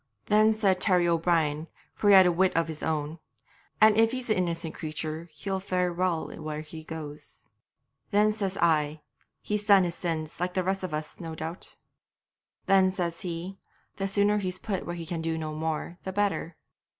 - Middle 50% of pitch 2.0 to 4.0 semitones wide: Yes, average, 3.3 semitones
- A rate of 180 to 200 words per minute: Yes, average, 185 wpm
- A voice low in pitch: No, medium, 175 Hz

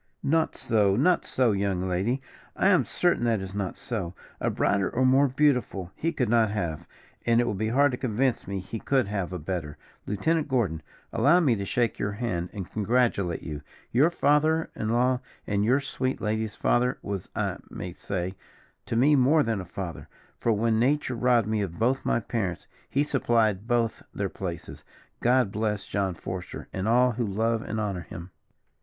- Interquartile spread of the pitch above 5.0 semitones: No, average, 4.6 semitones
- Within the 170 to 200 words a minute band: Yes, average, 190 wpm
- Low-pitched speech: Yes, low, 110 Hz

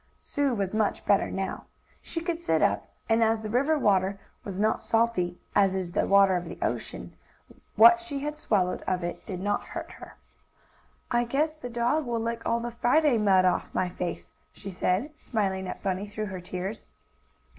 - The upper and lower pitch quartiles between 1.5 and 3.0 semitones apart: No, average, 4.2 semitones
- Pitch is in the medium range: No, high, 215 Hz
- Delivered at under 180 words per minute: No, average, 190 wpm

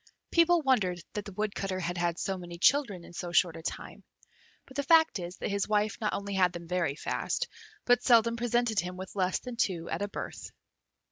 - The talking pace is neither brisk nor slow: No, fast, 210 wpm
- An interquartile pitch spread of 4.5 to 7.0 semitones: Yes, average, 4.8 semitones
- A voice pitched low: No, high, 200 Hz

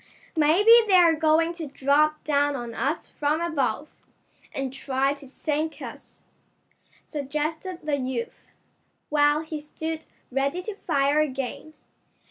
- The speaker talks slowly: Yes, slow, 120 wpm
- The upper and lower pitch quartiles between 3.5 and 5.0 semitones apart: No, narrow, 2.5 semitones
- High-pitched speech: Yes, very high, 300 Hz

